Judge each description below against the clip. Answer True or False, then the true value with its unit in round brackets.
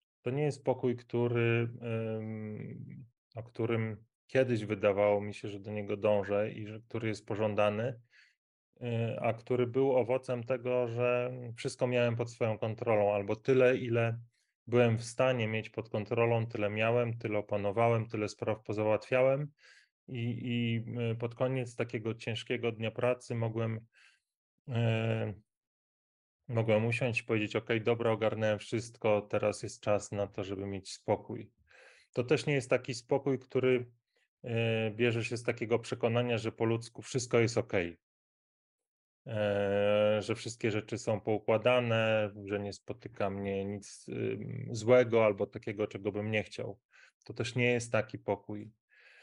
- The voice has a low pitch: True (115 Hz)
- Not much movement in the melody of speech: True (2.3 semitones)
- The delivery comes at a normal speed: True (140 wpm)